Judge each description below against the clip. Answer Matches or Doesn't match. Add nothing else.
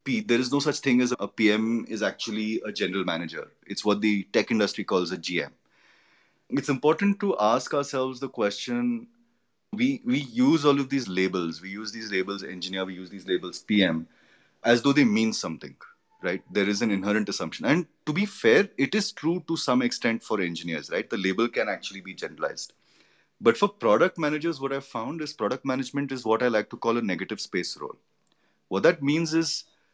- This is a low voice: Matches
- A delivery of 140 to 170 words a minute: Doesn't match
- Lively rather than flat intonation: Matches